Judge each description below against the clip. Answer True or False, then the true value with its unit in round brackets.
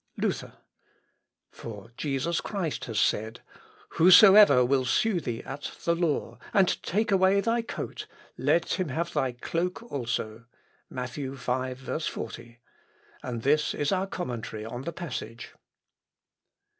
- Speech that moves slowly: True (125 wpm)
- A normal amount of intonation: False (6.7 semitones)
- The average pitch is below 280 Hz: True (140 Hz)